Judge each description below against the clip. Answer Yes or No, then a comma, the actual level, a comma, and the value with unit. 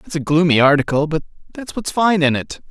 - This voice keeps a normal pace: No, fast, 220 wpm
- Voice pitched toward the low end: No, medium, 160 Hz